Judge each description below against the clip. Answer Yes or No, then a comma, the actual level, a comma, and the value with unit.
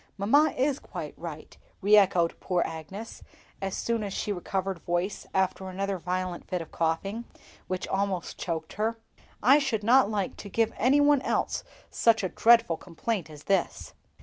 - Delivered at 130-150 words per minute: No, average, 165 wpm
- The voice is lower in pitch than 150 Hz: No, high, 195 Hz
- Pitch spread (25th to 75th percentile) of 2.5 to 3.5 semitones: No, average, 4.0 semitones